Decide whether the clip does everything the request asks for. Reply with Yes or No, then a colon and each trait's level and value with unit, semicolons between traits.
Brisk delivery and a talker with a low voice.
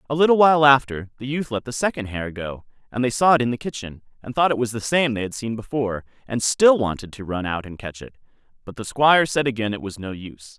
Yes: fast, 260 wpm; low, 120 Hz